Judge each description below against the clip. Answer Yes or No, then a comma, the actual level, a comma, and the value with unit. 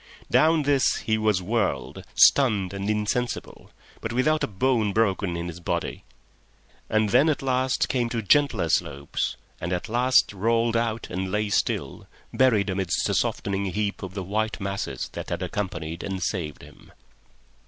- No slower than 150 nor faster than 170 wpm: Yes, average, 160 wpm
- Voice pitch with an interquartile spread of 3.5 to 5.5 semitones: Yes, average, 4.2 semitones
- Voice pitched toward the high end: No, low, 105 Hz